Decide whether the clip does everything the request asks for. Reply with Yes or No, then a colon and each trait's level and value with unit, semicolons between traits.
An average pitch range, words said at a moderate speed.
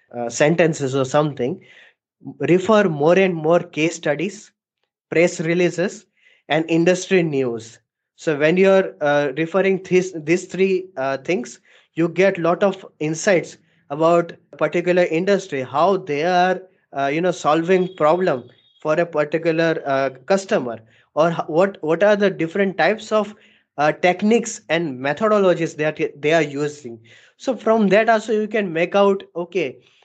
Yes: average, 4.0 semitones; average, 145 wpm